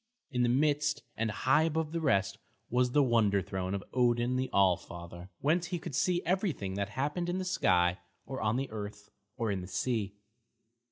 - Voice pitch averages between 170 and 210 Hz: No, low, 120 Hz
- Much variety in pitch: Yes, wide, 7.0 semitones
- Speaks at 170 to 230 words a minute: Yes, average, 190 wpm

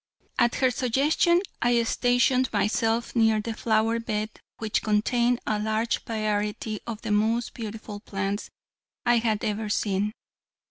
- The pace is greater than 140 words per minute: No, slow, 135 wpm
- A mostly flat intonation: Yes, narrow, 2.0 semitones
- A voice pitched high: Yes, high, 225 Hz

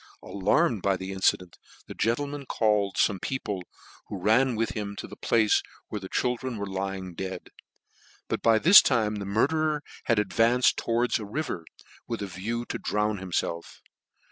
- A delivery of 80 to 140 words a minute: No, average, 165 wpm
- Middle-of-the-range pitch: No, low, 105 Hz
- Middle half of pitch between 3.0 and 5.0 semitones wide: Yes, average, 3.7 semitones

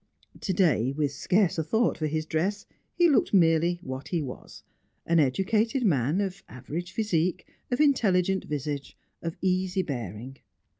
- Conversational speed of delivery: Yes, average, 150 wpm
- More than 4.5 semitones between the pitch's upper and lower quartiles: Yes, average, 5.0 semitones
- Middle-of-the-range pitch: Yes, medium, 170 Hz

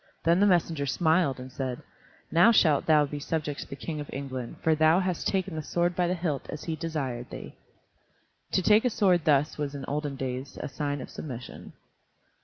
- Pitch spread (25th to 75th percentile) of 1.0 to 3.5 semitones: No, average, 3.9 semitones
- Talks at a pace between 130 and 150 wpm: No, fast, 205 wpm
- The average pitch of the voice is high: No, medium, 150 Hz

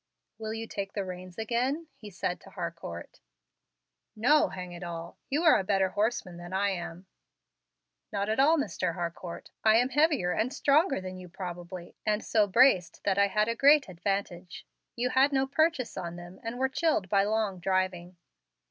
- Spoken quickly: No, average, 180 wpm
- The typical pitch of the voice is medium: No, high, 200 Hz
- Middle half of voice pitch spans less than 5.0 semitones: No, wide, 5.4 semitones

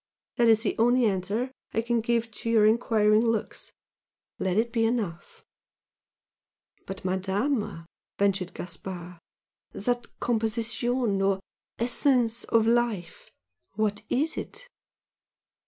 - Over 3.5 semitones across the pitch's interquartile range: No, average, 3.2 semitones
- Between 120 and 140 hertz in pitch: No, high, 225 Hz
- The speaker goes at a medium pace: No, slow, 110 wpm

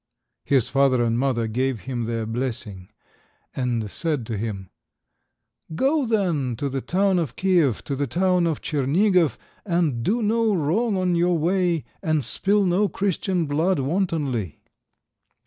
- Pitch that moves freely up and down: Yes, wide, 6.8 semitones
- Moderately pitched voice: Yes, medium, 150 Hz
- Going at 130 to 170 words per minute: Yes, average, 145 wpm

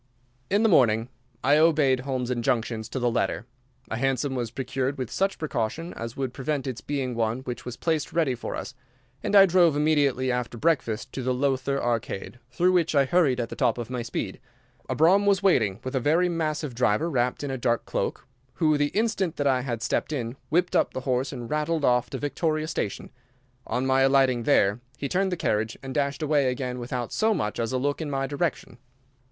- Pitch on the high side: No, low, 135 Hz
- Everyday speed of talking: No, fast, 210 wpm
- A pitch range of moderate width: Yes, average, 4.0 semitones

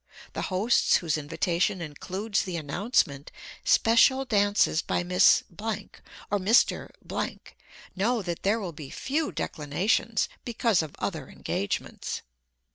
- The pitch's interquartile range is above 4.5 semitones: Yes, average, 5.1 semitones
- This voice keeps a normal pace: No, slow, 120 wpm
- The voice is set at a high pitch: Yes, high, 195 Hz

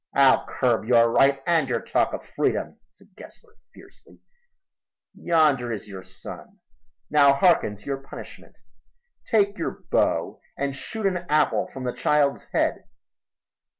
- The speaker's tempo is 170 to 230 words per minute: No, average, 140 wpm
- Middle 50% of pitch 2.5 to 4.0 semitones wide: No, average, 5.1 semitones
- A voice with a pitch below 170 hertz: Yes, medium, 140 Hz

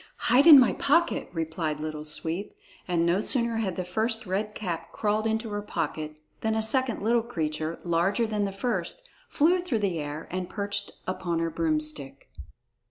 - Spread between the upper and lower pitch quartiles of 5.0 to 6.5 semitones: Yes, average, 5.3 semitones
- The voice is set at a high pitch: Yes, high, 195 Hz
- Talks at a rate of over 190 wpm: No, average, 170 wpm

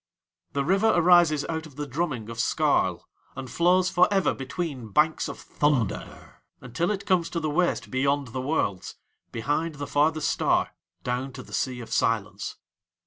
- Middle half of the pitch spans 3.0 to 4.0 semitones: No, average, 4.8 semitones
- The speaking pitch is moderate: Yes, medium, 150 Hz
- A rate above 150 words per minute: Yes, average, 165 wpm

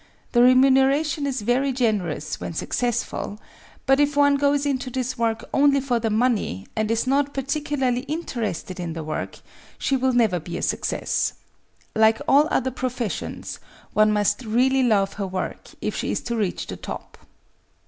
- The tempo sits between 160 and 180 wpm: Yes, average, 170 wpm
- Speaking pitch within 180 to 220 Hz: No, high, 245 Hz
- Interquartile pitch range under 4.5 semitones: Yes, average, 4.1 semitones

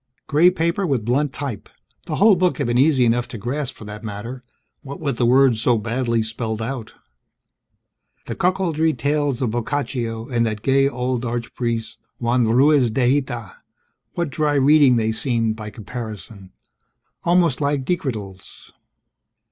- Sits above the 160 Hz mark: No, low, 125 Hz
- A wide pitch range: No, average, 4.0 semitones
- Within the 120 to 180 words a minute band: Yes, average, 150 wpm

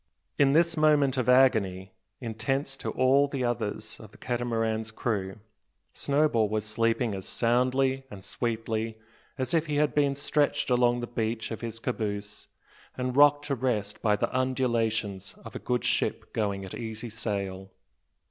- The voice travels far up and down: No, average, 3.5 semitones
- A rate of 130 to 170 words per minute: Yes, average, 155 wpm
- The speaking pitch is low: Yes, low, 120 Hz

